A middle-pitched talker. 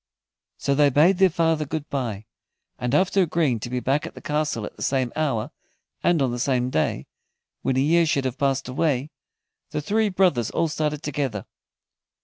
Yes: medium, 145 Hz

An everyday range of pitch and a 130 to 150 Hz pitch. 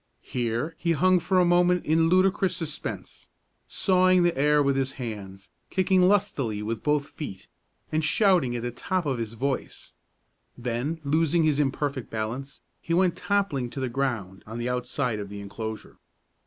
No: wide, 6.6 semitones; medium, 140 Hz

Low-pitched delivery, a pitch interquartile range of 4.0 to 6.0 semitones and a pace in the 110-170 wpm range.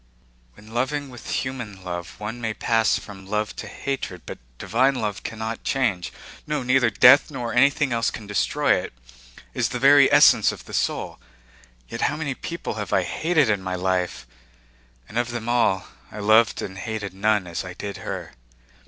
No: low, 110 Hz; average, 4.4 semitones; average, 180 wpm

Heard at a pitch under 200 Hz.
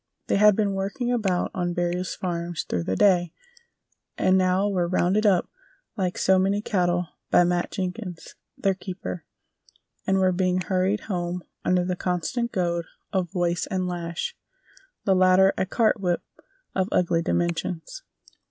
Yes: medium, 185 Hz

